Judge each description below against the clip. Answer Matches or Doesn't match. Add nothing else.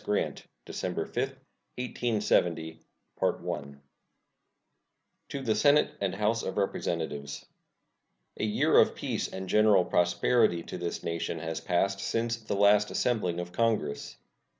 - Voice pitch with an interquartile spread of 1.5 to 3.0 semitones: Doesn't match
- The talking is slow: Matches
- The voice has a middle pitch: Doesn't match